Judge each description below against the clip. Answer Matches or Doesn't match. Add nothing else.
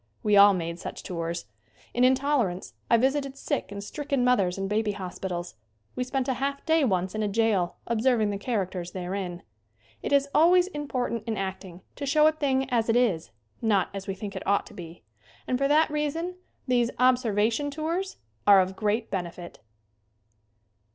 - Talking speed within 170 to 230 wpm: Matches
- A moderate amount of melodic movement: Doesn't match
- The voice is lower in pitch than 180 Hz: Doesn't match